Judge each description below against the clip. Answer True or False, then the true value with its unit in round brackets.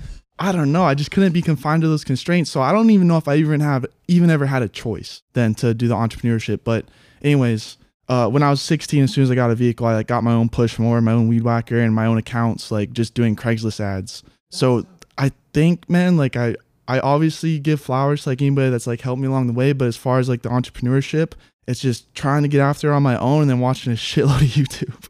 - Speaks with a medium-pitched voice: False (130 Hz)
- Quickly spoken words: True (255 wpm)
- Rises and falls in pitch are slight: False (3.8 semitones)